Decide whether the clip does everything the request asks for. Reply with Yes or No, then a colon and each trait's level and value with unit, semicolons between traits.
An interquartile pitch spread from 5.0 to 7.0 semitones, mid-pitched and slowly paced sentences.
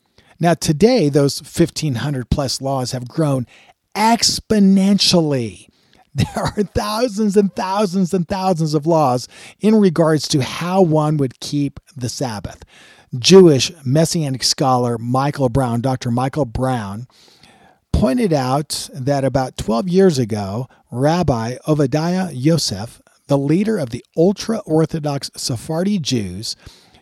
Yes: wide, 5.5 semitones; medium, 145 Hz; slow, 120 wpm